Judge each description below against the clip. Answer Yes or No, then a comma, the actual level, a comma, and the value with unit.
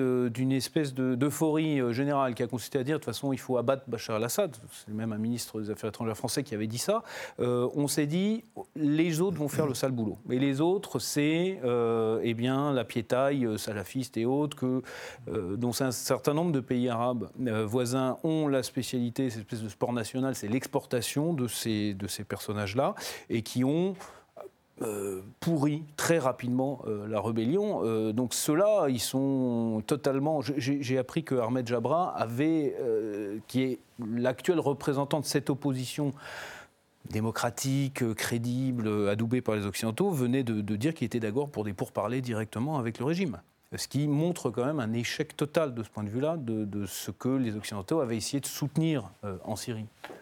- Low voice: Yes, low, 125 Hz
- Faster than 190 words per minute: No, average, 185 wpm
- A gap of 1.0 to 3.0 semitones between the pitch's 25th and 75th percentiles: No, average, 4.2 semitones